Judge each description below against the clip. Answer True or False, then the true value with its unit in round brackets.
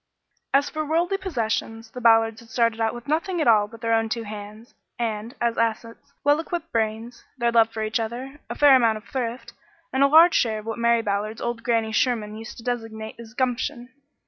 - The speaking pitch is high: True (230 Hz)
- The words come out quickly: True (210 wpm)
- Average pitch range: False (2.3 semitones)